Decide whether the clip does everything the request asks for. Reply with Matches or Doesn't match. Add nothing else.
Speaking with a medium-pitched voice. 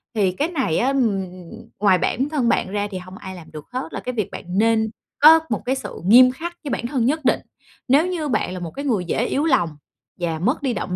Doesn't match